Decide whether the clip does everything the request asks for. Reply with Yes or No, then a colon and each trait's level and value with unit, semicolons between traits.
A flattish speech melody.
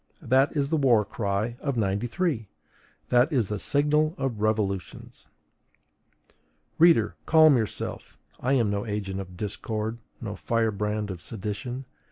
No: average, 4.6 semitones